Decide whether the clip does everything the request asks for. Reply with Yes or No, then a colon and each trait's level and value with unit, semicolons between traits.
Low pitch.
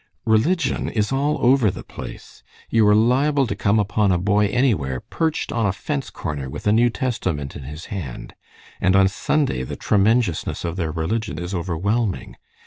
Yes: low, 105 Hz